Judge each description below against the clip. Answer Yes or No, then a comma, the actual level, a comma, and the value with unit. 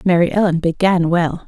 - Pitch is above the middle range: No, medium, 175 Hz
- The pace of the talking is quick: No, average, 165 wpm